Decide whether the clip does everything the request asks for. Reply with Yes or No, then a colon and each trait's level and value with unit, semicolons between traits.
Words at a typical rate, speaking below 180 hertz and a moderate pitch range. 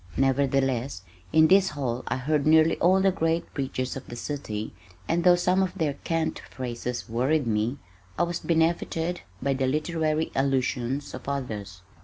Yes: average, 160 wpm; medium, 140 Hz; average, 4.2 semitones